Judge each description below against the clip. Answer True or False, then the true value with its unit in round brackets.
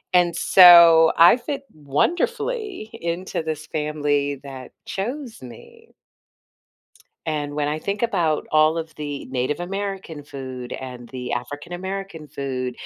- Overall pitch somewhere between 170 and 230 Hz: False (155 Hz)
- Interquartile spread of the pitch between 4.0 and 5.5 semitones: True (5.1 semitones)